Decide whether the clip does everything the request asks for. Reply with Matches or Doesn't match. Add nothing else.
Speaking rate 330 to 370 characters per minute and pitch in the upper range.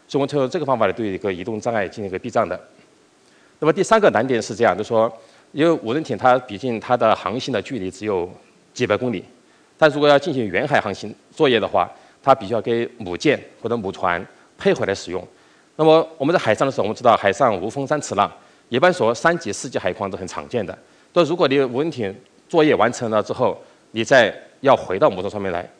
Doesn't match